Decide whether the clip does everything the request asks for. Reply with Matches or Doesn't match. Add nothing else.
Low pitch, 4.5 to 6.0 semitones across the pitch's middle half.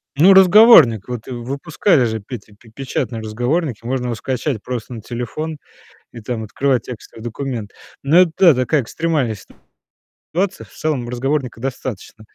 Matches